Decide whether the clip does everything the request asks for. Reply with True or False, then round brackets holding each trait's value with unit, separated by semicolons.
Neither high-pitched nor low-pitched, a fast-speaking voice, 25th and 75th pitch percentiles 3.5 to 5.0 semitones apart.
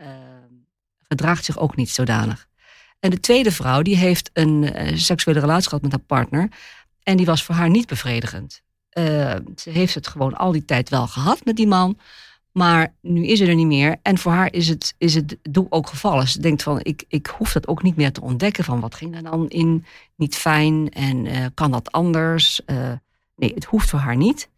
True (160 Hz; 220 wpm; 4.5 semitones)